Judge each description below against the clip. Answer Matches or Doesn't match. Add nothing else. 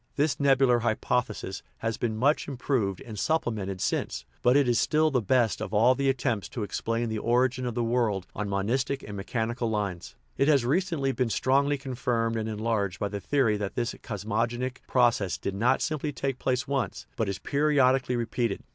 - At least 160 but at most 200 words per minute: Matches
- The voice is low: Matches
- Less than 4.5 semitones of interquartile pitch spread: Matches